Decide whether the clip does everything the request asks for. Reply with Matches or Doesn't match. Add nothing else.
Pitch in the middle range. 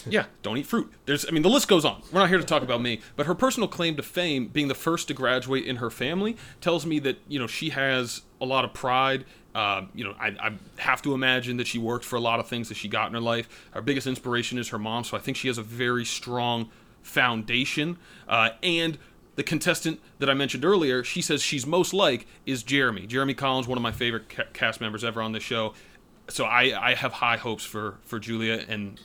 Doesn't match